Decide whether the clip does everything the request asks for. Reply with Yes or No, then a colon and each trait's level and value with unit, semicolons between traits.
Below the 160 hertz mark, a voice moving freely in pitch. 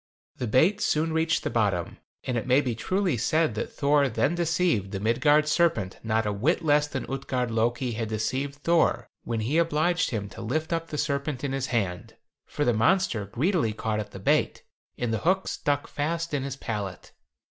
Yes: low, 135 Hz; wide, 6.0 semitones